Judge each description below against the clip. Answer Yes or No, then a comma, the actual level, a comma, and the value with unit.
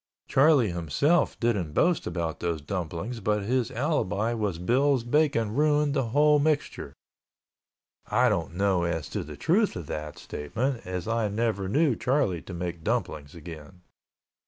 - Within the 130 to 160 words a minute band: Yes, average, 150 wpm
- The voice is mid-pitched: No, low, 110 Hz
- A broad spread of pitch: Yes, wide, 7.9 semitones